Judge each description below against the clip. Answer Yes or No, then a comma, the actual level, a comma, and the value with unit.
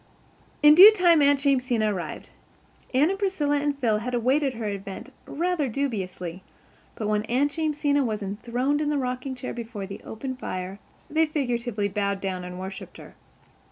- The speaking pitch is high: Yes, very high, 250 Hz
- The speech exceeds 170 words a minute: No, average, 165 wpm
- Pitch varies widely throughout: Yes, wide, 5.7 semitones